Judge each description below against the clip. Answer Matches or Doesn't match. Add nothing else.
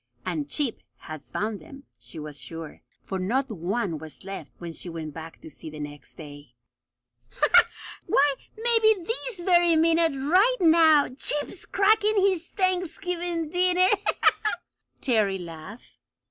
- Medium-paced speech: Doesn't match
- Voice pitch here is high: Matches